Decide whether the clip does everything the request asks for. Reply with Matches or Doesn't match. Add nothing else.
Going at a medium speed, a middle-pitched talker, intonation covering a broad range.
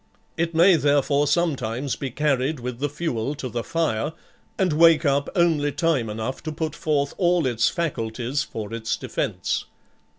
Doesn't match